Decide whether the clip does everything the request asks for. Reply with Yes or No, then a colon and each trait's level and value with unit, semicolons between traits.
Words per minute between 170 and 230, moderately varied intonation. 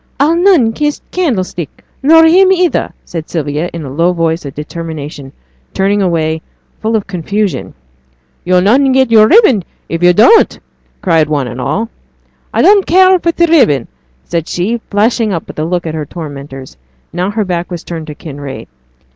No: average, 175 wpm; wide, 7.1 semitones